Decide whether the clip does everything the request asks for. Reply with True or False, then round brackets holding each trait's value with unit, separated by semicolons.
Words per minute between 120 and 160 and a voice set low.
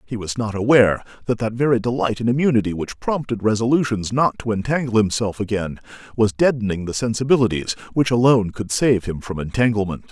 False (170 wpm; 115 Hz)